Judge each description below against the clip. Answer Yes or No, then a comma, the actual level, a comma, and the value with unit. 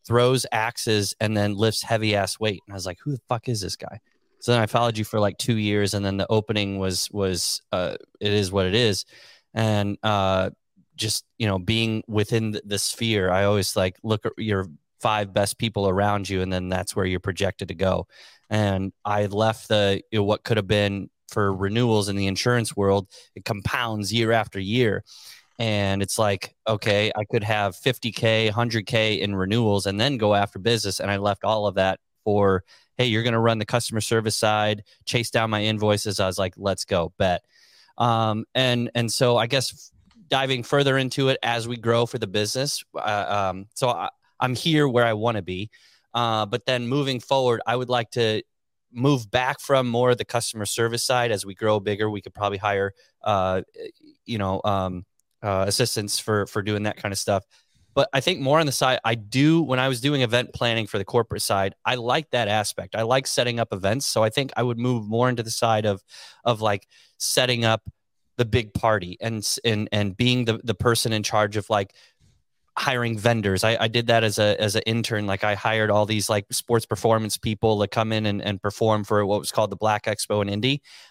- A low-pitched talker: Yes, low, 110 Hz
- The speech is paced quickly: Yes, fast, 215 wpm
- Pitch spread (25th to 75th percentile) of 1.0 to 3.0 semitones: Yes, average, 2.7 semitones